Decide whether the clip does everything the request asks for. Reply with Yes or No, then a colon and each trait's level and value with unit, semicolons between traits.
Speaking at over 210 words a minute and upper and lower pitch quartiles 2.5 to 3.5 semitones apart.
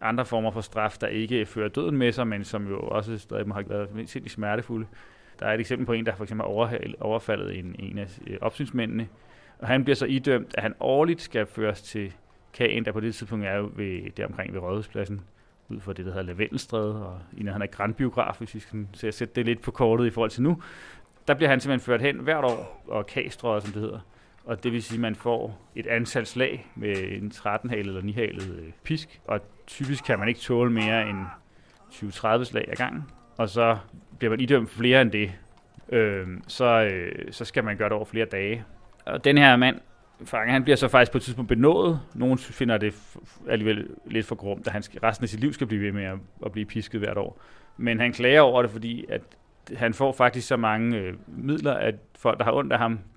Yes: fast, 225 wpm; average, 2.9 semitones